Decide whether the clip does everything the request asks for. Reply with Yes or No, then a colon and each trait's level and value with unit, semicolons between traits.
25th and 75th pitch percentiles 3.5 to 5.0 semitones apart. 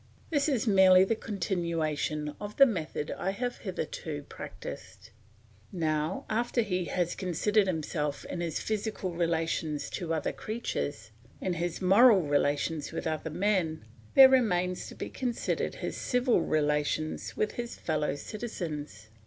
No: wide, 5.5 semitones